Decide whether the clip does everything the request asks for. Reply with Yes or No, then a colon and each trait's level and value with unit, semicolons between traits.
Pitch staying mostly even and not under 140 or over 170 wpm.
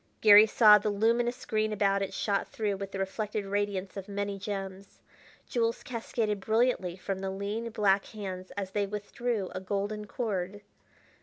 Yes: narrow, 1.8 semitones; average, 160 wpm